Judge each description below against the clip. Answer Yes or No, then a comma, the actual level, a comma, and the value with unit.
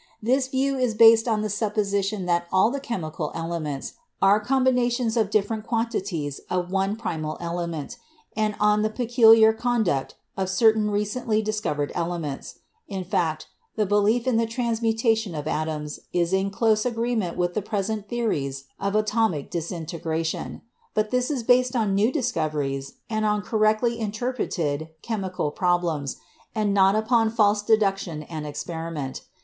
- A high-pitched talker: Yes, high, 210 Hz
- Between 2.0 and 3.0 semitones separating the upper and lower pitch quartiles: No, average, 4.8 semitones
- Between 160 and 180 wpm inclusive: No, average, 150 wpm